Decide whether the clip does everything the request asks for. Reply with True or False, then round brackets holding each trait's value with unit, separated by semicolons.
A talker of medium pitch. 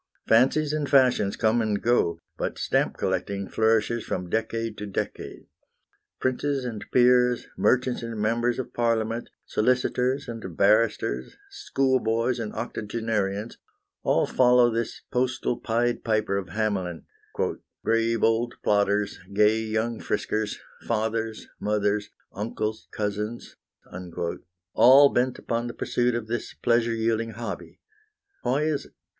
False (115 Hz)